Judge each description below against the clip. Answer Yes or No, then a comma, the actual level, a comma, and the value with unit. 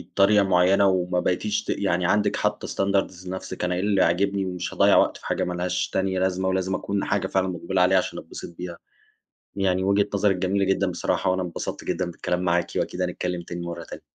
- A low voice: Yes, very low, 95 Hz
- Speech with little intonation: Yes, narrow, 1.6 semitones